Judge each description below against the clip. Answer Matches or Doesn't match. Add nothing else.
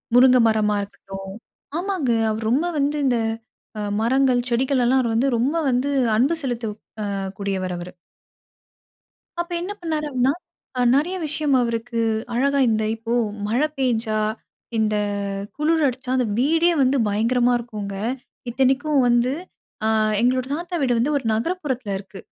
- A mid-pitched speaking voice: Doesn't match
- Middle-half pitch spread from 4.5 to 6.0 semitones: Doesn't match